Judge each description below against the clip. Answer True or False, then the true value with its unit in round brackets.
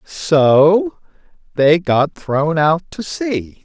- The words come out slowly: True (115 wpm)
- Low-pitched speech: False (165 Hz)